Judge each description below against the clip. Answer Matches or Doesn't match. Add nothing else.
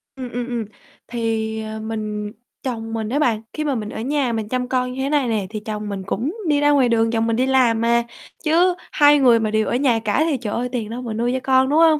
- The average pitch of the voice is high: Matches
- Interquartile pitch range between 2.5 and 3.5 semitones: Matches